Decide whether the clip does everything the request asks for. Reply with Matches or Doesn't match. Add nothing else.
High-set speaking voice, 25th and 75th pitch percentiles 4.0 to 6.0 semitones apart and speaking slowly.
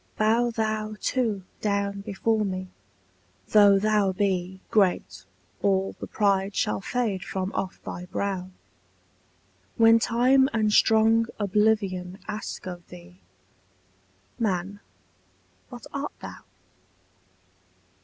Doesn't match